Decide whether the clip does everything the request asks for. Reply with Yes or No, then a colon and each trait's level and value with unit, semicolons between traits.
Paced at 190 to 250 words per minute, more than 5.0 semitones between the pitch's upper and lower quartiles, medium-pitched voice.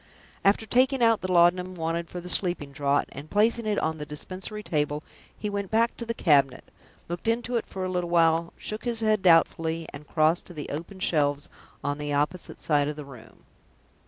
Yes: average, 200 wpm; wide, 5.6 semitones; medium, 175 Hz